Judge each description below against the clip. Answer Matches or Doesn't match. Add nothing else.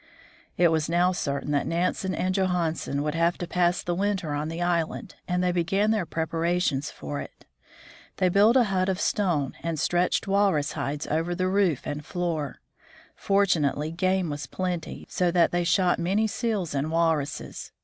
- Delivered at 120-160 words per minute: Doesn't match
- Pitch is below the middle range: Doesn't match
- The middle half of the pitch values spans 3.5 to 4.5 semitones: Doesn't match